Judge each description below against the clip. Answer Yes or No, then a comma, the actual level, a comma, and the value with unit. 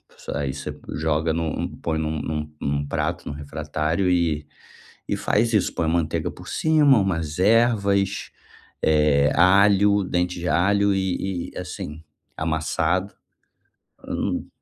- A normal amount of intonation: Yes, average, 4.1 semitones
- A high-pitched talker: No, very low, 85 Hz